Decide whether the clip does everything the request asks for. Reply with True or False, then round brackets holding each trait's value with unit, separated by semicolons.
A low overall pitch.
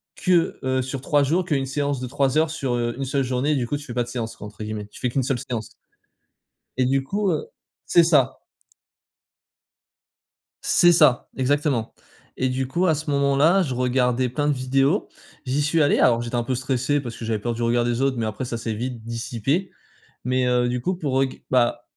True (130 Hz)